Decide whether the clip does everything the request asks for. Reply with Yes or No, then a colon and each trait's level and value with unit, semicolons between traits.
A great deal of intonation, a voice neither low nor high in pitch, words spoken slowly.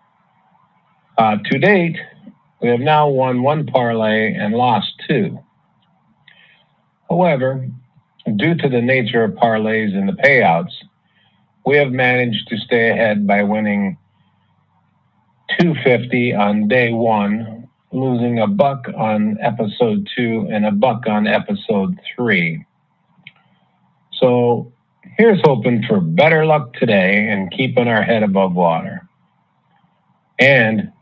No: wide, 5.9 semitones; low, 125 Hz; slow, 115 wpm